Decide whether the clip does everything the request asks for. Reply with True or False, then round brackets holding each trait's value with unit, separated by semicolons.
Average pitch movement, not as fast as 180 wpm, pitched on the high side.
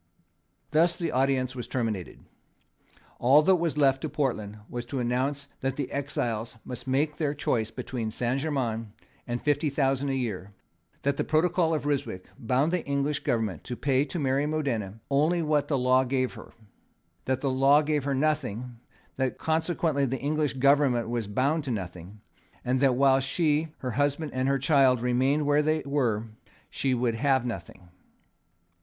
False (3.1 semitones; 170 wpm; 135 Hz)